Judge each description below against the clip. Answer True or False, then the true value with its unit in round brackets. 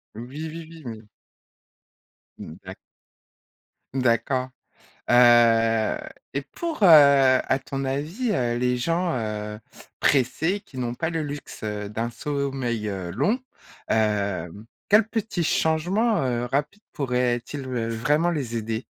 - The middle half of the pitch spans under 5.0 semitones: False (5.5 semitones)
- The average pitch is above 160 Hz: False (130 Hz)